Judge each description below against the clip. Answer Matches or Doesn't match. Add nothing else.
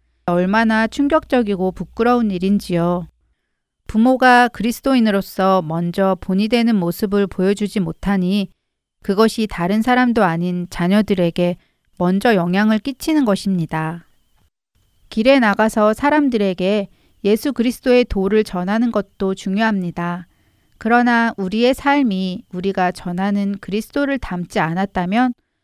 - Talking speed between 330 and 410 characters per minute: Doesn't match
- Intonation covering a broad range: Doesn't match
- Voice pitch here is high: Matches